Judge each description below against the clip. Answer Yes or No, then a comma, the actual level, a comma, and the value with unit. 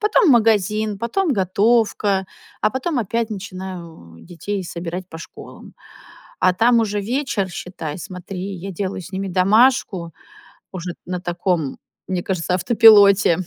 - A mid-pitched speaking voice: No, high, 195 Hz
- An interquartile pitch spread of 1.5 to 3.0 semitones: No, average, 3.7 semitones